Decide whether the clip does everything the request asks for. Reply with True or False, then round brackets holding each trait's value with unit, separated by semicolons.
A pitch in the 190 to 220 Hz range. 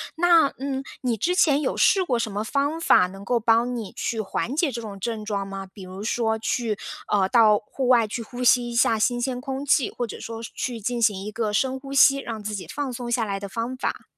False (235 Hz)